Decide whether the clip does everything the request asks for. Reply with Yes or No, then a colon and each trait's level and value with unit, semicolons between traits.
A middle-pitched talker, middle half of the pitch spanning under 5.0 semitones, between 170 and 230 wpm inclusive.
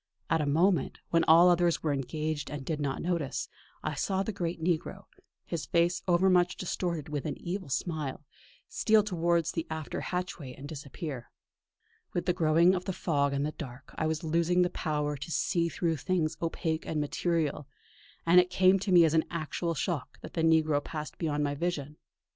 Yes: medium, 165 Hz; average, 2.8 semitones; average, 190 wpm